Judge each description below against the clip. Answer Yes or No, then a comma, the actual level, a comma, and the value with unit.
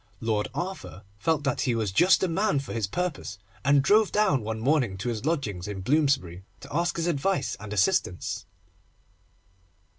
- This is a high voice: No, low, 135 Hz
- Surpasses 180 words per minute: No, average, 170 wpm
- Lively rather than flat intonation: Yes, wide, 8.2 semitones